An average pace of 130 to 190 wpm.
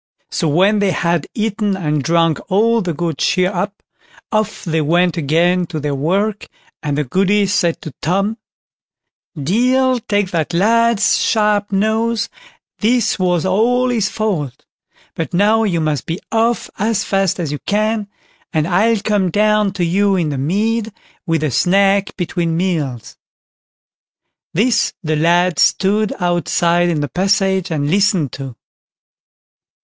Yes: average, 145 wpm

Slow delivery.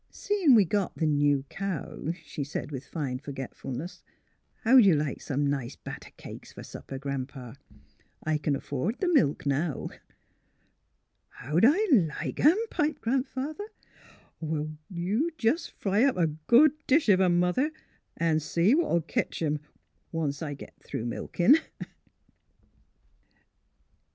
No: average, 155 wpm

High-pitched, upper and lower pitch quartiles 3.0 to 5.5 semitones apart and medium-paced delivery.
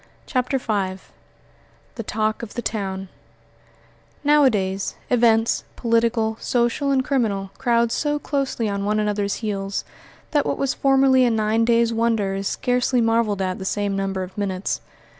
Yes: high, 225 Hz; average, 3.7 semitones; average, 145 wpm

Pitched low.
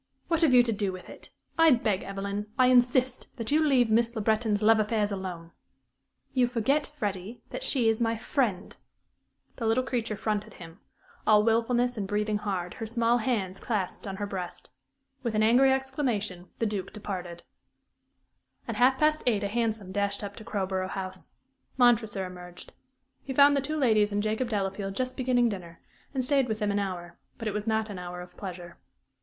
No: high, 215 Hz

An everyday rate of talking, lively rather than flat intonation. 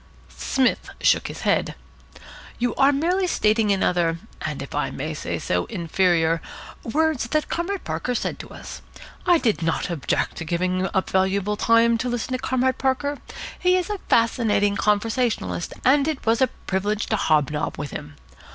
Yes: average, 170 wpm; wide, 6.3 semitones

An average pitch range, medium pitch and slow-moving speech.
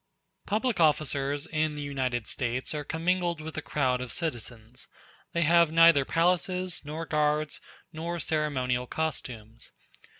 Yes: average, 4.2 semitones; medium, 150 Hz; slow, 130 wpm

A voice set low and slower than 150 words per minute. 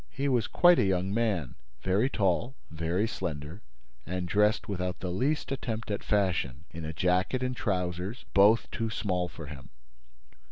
No: very low, 95 Hz; average, 160 wpm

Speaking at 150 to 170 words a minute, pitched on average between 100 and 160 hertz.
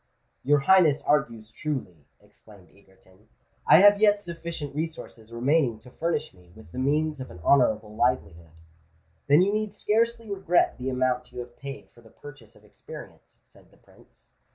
Yes: average, 165 wpm; low, 135 Hz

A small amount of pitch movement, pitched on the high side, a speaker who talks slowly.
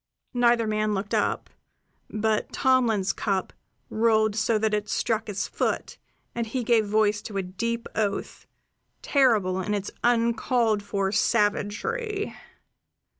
Yes: narrow, 2.2 semitones; high, 215 Hz; slow, 125 wpm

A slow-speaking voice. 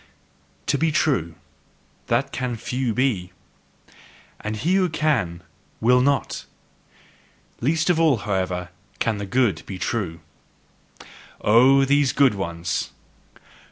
Yes: slow, 115 wpm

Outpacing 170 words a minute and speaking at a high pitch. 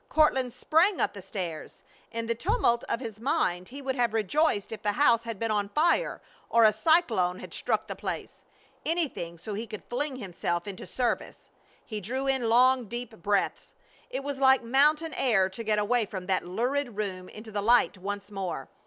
Yes: average, 190 wpm; high, 230 Hz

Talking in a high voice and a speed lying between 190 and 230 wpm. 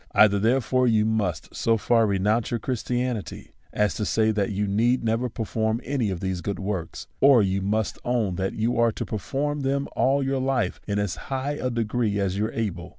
No: low, 110 Hz; fast, 205 wpm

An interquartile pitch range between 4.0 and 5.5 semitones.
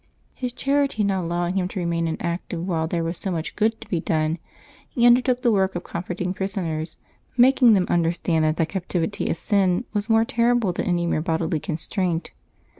Yes: average, 4.4 semitones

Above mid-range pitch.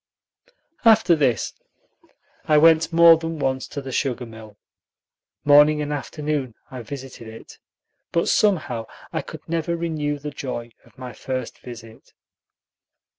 No: medium, 145 Hz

